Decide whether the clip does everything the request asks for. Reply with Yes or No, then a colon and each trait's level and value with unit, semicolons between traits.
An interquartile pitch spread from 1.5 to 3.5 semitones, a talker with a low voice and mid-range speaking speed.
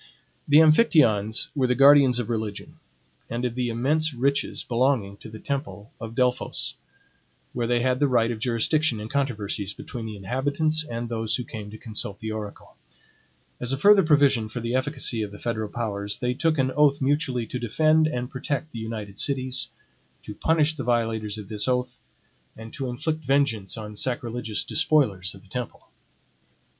No: average, 4.1 semitones; low, 120 Hz; average, 175 wpm